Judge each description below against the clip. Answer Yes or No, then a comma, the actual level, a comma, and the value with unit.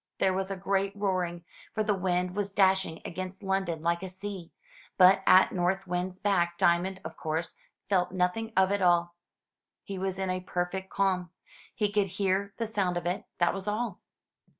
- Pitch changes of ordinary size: No, narrow, 1.7 semitones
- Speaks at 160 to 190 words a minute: Yes, average, 180 wpm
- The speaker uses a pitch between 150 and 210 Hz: Yes, high, 190 Hz